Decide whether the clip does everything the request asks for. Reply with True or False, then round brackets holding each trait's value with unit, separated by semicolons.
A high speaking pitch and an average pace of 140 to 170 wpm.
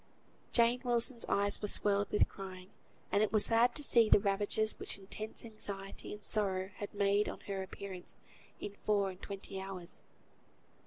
True (205 Hz; 165 wpm)